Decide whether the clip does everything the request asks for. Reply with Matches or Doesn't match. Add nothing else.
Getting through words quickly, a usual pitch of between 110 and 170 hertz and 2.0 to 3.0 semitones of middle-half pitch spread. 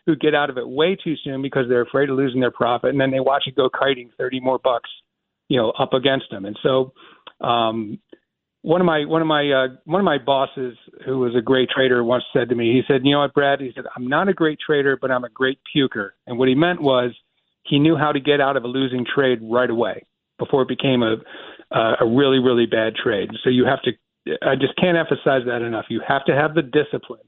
Matches